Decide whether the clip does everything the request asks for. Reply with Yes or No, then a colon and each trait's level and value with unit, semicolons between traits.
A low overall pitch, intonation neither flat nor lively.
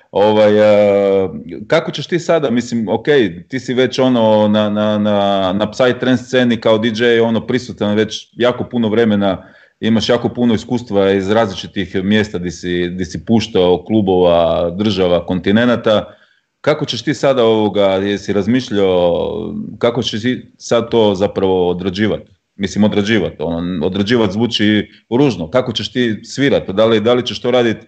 Yes: low, 110 Hz; average, 3.3 semitones